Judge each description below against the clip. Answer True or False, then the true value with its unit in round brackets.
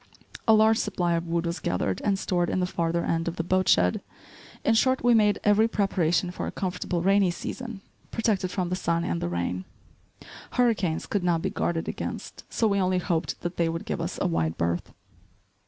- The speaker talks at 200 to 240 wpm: True (205 wpm)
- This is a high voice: False (180 Hz)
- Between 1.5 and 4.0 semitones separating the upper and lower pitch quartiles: True (3.4 semitones)